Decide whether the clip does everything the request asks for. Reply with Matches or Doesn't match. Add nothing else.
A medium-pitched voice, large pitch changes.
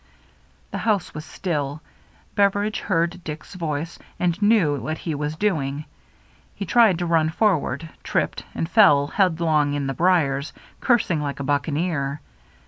Doesn't match